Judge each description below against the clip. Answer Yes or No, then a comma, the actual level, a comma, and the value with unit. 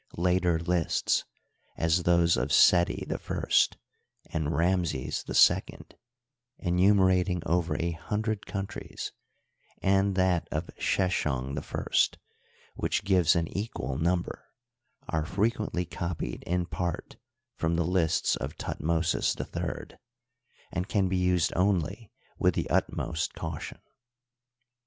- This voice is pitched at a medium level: No, very low, 90 Hz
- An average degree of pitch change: No, narrow, 2.3 semitones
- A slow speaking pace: Yes, slow, 115 wpm